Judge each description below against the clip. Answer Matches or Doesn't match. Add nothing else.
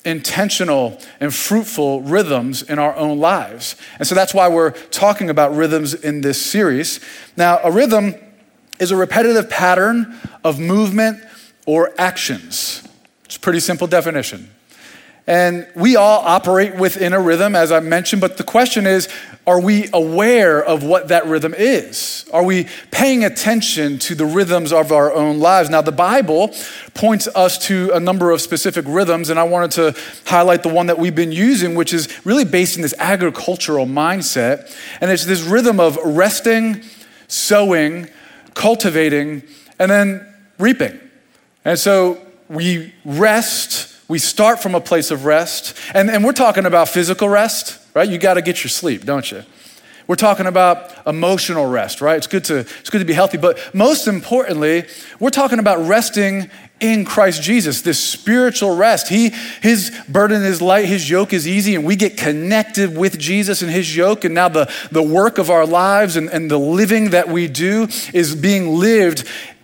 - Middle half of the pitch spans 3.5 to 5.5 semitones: Matches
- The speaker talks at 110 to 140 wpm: Doesn't match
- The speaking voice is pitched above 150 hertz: Matches